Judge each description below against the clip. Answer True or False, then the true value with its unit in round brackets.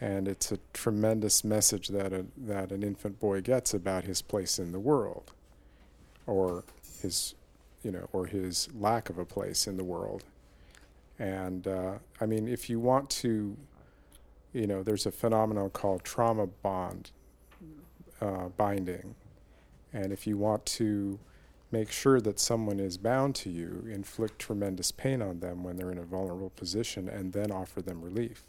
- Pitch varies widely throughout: False (2.8 semitones)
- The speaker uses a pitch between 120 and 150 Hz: False (100 Hz)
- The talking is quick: False (165 wpm)